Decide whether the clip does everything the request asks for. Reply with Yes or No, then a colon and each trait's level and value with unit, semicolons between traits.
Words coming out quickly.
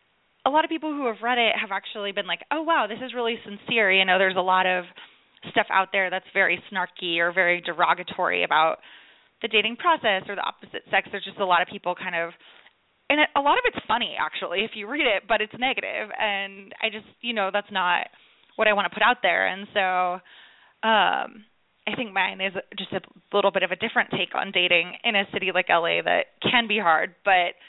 Yes: fast, 225 wpm